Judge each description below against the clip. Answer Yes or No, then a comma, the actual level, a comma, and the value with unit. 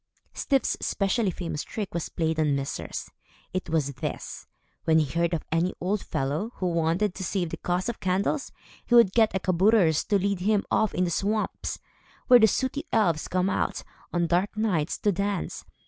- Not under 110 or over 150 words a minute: No, average, 185 wpm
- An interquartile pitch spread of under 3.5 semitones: No, average, 4.0 semitones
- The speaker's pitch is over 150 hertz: Yes, medium, 185 Hz